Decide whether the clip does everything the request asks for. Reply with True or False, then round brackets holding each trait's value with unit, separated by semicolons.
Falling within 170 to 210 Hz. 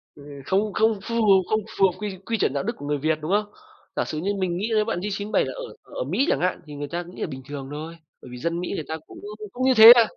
True (190 Hz)